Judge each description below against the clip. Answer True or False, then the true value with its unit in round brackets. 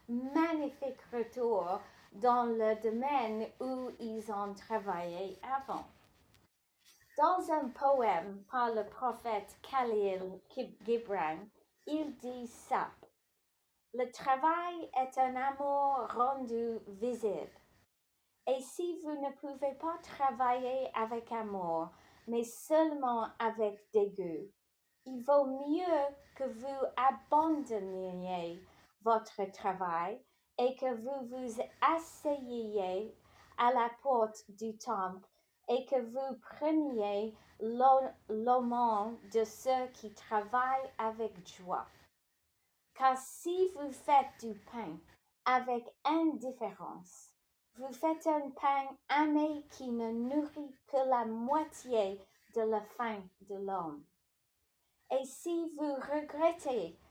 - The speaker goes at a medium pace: False (105 wpm)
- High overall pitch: True (245 Hz)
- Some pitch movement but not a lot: True (4.1 semitones)